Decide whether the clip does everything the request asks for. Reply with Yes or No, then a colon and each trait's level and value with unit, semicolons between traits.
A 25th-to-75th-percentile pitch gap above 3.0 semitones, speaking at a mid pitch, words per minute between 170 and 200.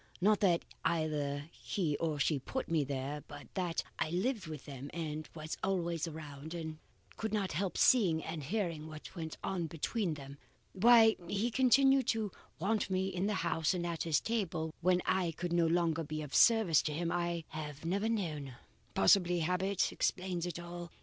Yes: average, 3.6 semitones; medium, 170 Hz; average, 175 wpm